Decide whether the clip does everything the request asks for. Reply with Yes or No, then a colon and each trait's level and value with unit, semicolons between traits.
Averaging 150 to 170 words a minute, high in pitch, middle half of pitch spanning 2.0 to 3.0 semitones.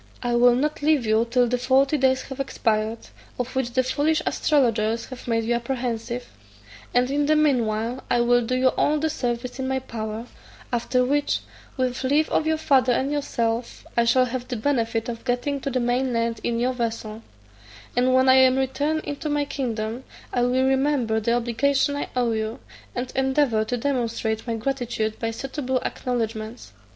No: average, 185 wpm; very high, 250 Hz; narrow, 2.4 semitones